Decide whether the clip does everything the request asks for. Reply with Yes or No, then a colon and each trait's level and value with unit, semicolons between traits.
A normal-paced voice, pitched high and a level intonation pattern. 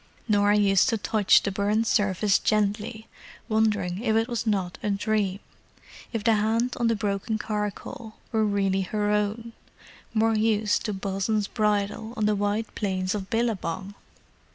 Yes: average, 150 wpm; high, 210 Hz; narrow, 1.7 semitones